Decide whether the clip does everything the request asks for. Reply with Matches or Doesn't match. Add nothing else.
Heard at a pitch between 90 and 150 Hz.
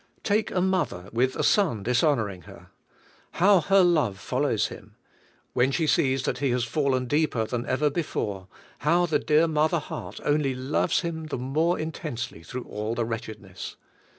Matches